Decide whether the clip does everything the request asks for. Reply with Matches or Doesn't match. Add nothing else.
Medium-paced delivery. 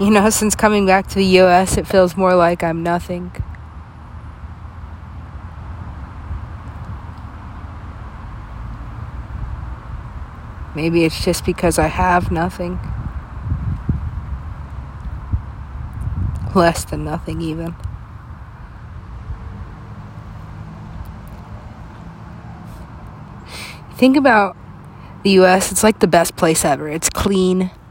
Doesn't match